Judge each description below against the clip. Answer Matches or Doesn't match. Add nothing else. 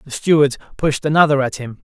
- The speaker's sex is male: Matches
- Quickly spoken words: Doesn't match